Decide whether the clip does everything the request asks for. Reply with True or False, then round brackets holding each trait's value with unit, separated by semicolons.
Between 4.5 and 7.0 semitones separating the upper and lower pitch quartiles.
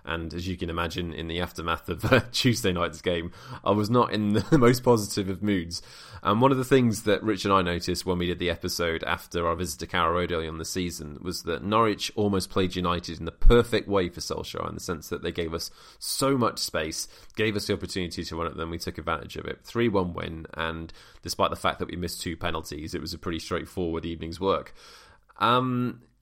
False (3.9 semitones)